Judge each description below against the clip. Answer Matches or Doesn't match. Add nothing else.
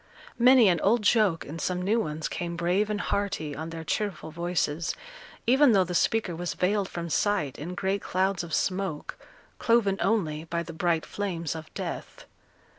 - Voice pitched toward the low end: Doesn't match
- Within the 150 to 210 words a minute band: Matches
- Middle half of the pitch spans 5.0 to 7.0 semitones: Doesn't match